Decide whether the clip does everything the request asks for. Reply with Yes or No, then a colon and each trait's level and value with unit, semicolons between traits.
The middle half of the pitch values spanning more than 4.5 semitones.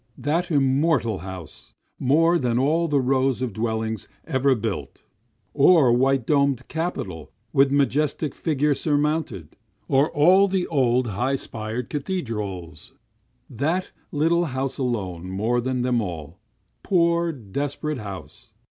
Yes: average, 5.2 semitones